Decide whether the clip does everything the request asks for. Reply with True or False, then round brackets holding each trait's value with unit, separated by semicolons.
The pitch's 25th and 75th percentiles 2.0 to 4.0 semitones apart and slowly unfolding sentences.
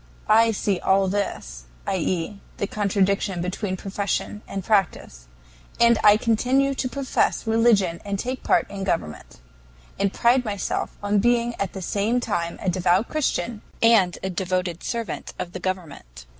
False (3.7 semitones; 155 wpm)